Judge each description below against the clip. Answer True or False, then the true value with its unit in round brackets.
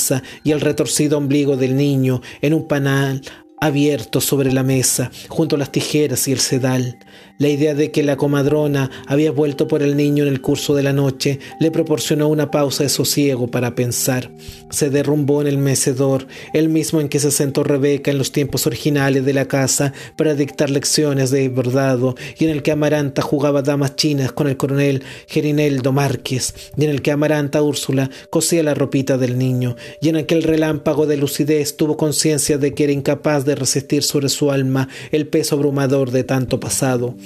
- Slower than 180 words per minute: False (185 wpm)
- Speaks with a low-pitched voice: False (145 Hz)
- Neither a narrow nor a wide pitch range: False (2.0 semitones)